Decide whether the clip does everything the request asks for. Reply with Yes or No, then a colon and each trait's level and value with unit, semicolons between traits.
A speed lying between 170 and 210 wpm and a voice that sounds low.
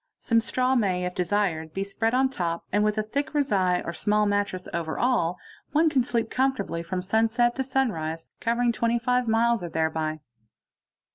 No: average, 180 wpm; high, 210 Hz